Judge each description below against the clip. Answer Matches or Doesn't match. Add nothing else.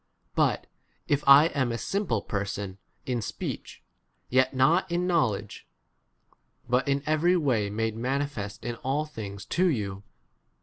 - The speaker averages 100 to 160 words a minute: Matches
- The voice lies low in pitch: Matches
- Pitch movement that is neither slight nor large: Doesn't match